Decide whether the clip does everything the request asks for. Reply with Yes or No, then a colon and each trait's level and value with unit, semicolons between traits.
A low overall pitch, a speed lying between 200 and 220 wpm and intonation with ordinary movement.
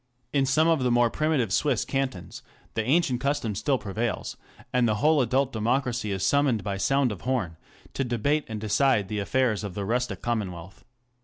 No: low, 120 Hz; average, 175 wpm; average, 4.5 semitones